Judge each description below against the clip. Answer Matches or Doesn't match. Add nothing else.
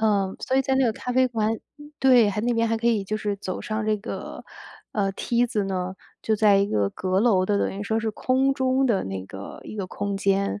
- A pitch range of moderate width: Matches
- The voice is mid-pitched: Doesn't match